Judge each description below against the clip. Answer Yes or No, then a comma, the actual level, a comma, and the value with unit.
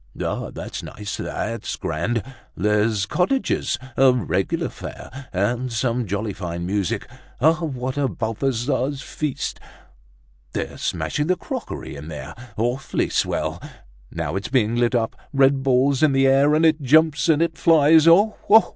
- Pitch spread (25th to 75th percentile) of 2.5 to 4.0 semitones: No, average, 5.2 semitones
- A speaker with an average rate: Yes, average, 145 wpm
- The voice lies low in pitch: Yes, low, 130 Hz